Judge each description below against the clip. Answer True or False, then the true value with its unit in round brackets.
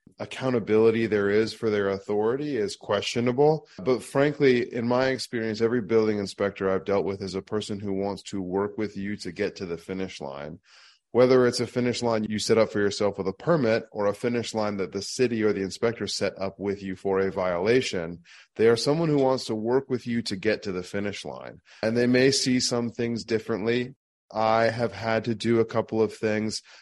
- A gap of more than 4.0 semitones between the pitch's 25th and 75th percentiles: False (3.2 semitones)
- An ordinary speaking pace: False (215 wpm)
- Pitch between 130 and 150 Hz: False (110 Hz)